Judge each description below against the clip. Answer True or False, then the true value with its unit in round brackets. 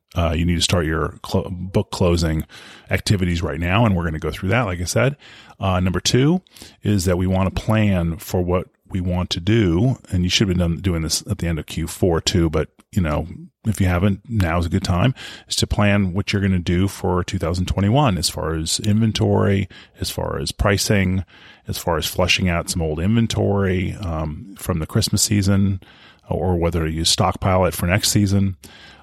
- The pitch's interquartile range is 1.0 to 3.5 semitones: True (3.2 semitones)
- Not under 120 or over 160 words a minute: False (205 wpm)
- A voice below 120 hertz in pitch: True (95 Hz)